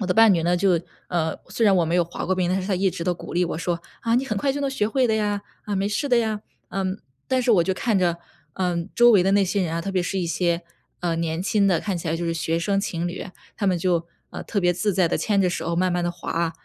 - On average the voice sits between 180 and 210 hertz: Yes, medium, 185 Hz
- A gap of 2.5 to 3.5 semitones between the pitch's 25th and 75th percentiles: Yes, average, 3.1 semitones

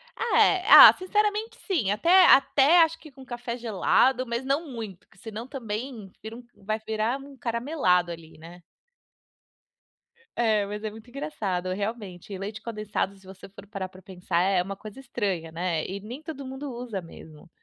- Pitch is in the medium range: No, high, 220 Hz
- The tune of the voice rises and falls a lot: Yes, wide, 5.7 semitones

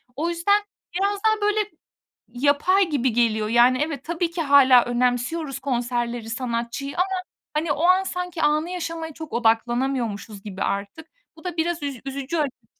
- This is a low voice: No, very high, 280 Hz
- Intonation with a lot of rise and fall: Yes, wide, 5.8 semitones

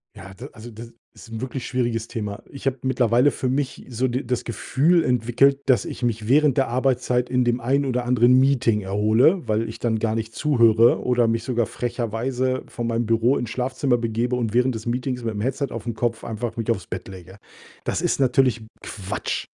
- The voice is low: Yes, low, 120 Hz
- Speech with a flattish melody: Yes, narrow, 2.3 semitones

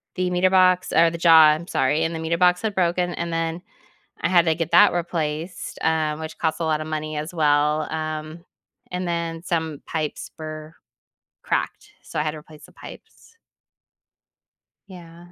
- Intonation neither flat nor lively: No, narrow, 1.9 semitones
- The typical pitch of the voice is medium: Yes, medium, 165 Hz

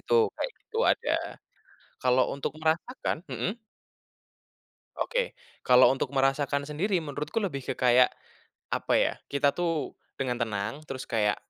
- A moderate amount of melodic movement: Yes, average, 4.2 semitones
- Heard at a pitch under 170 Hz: Yes, medium, 140 Hz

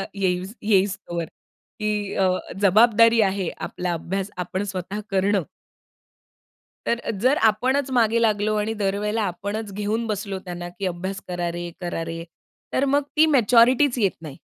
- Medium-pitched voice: No, high, 200 Hz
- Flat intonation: No, average, 3.4 semitones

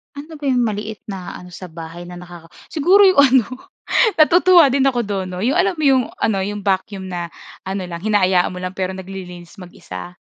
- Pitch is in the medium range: No, high, 195 Hz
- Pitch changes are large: Yes, wide, 6.6 semitones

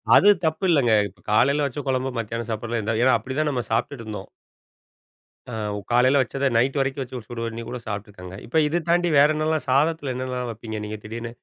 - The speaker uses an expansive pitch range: No, average, 3.8 semitones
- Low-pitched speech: Yes, low, 125 Hz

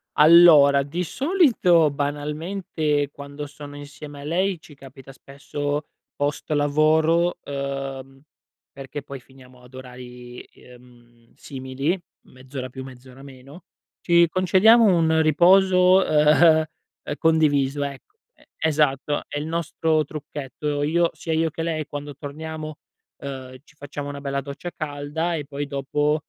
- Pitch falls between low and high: Yes, medium, 145 Hz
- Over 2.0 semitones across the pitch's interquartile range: Yes, narrow, 2.6 semitones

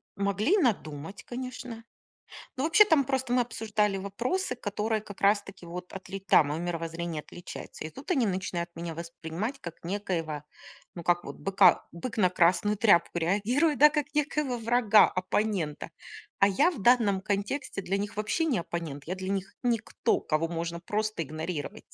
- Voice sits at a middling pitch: No, high, 200 Hz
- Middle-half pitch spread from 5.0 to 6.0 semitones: Yes, wide, 5.5 semitones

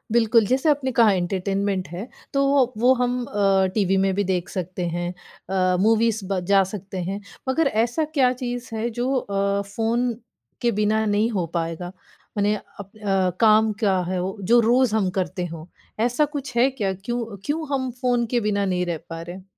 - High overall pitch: Yes, high, 205 Hz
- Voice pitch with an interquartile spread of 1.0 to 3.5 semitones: No, average, 4.1 semitones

